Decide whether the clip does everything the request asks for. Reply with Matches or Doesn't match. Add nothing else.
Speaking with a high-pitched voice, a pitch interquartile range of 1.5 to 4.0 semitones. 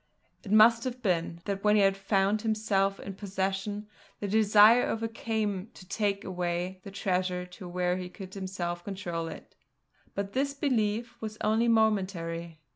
Matches